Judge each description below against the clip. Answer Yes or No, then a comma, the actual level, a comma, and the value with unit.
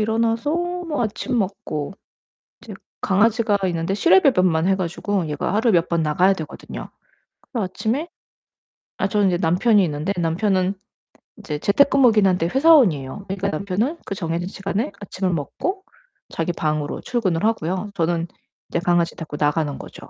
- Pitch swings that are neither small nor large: Yes, average, 4.9 semitones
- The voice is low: No, high, 190 Hz